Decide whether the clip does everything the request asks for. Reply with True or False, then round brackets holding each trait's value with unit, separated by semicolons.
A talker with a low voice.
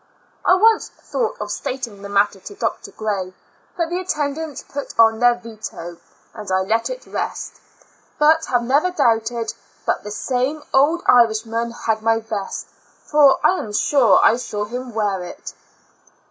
False (235 Hz)